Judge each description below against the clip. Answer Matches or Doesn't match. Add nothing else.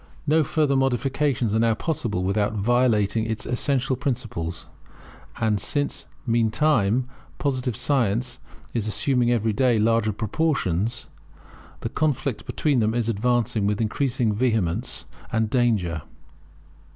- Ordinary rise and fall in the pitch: Matches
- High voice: Doesn't match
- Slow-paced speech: Matches